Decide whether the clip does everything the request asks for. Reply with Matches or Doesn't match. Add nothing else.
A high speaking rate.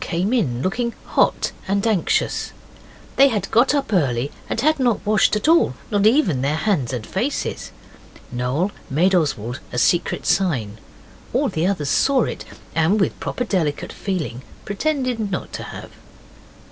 Doesn't match